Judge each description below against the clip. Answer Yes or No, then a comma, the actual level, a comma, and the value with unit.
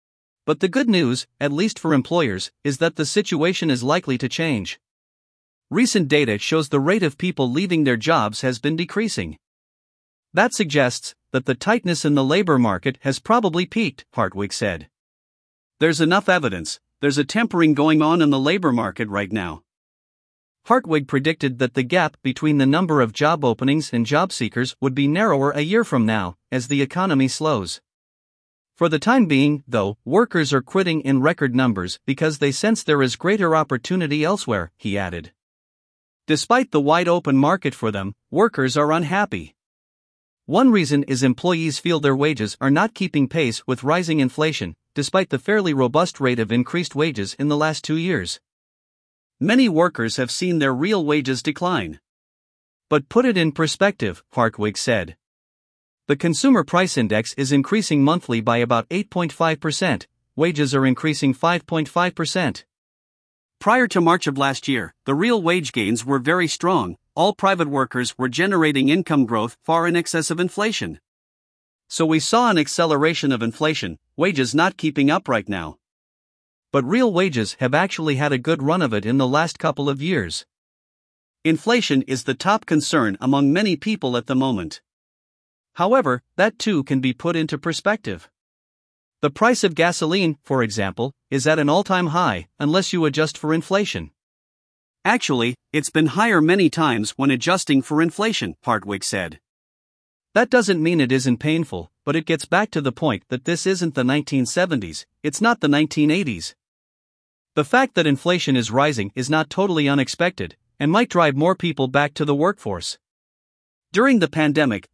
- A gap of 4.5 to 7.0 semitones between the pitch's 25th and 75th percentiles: Yes, average, 4.8 semitones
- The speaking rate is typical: Yes, average, 165 wpm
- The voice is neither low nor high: Yes, medium, 150 Hz